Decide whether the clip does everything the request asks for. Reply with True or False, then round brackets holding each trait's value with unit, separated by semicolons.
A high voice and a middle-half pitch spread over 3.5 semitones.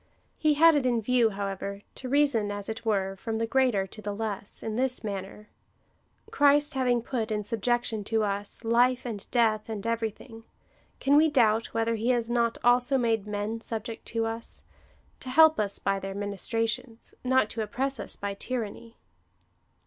False (225 Hz; 3.1 semitones)